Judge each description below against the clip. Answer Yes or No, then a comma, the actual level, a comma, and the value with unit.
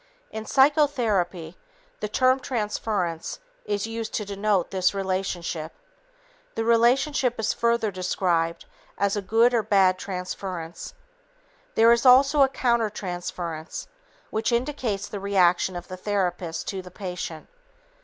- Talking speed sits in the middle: No, slow, 125 wpm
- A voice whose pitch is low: No, high, 200 Hz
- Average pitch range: Yes, average, 4.3 semitones